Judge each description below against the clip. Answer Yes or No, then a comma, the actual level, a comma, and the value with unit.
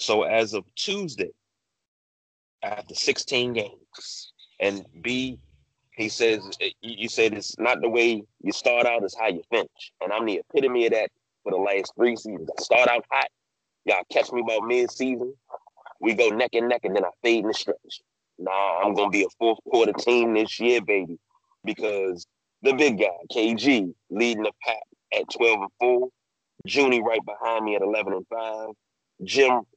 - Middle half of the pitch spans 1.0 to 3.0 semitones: Yes, narrow, 2.4 semitones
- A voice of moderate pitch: No, low, 115 Hz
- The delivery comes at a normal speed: Yes, average, 175 wpm